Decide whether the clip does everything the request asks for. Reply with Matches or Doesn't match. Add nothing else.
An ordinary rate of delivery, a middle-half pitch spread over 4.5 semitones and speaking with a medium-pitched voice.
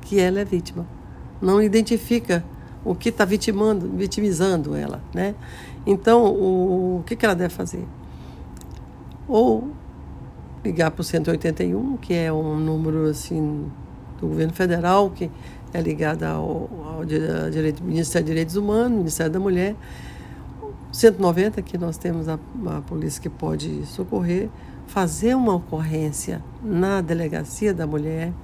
Doesn't match